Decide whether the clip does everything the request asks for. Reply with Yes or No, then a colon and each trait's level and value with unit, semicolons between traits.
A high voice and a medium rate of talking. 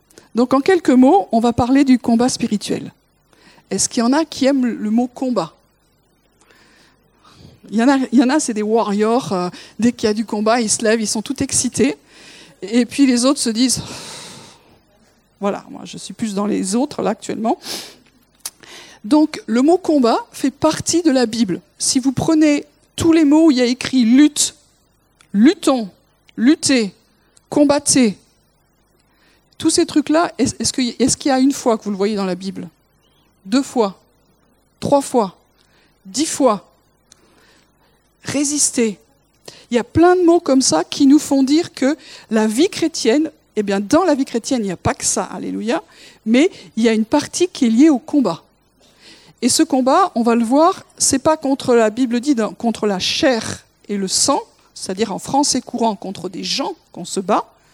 Yes: very high, 250 Hz; average, 185 wpm